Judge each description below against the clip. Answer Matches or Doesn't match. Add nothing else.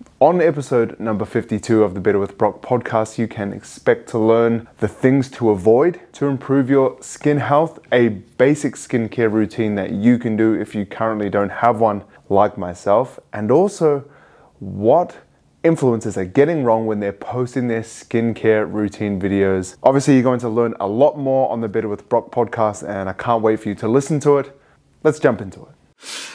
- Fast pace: Doesn't match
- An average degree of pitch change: Matches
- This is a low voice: Matches